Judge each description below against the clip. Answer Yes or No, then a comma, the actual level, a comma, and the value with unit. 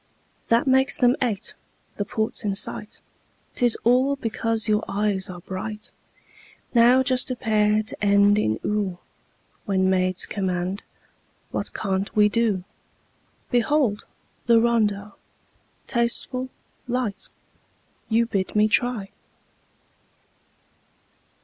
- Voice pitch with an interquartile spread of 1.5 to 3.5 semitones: Yes, average, 3.0 semitones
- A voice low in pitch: No, high, 215 Hz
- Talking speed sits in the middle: No, slow, 110 wpm